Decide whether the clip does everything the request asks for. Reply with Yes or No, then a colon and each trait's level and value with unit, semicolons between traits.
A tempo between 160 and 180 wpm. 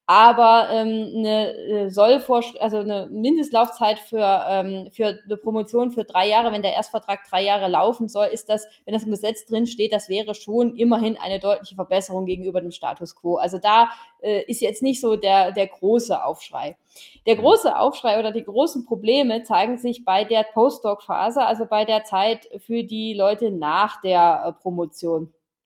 Yes: average, 175 wpm